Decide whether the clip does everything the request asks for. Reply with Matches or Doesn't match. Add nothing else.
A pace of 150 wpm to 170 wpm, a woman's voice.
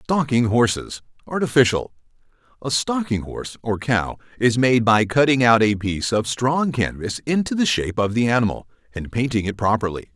Doesn't match